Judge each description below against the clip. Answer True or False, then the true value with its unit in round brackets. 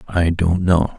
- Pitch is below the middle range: True (85 Hz)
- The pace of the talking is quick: False (185 wpm)